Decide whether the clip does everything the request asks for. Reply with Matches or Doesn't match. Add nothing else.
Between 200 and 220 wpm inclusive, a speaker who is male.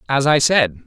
Matches